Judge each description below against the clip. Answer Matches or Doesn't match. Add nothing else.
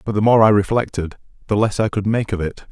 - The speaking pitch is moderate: Doesn't match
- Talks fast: Matches